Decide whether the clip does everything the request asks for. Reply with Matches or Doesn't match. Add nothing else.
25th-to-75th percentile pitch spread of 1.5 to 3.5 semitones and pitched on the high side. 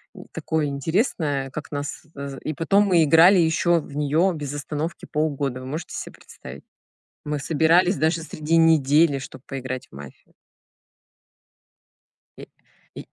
Doesn't match